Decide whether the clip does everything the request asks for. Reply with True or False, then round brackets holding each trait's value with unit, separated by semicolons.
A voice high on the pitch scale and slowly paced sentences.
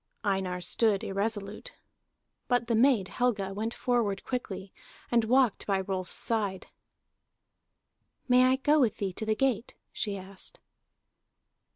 True (215 Hz; 130 wpm)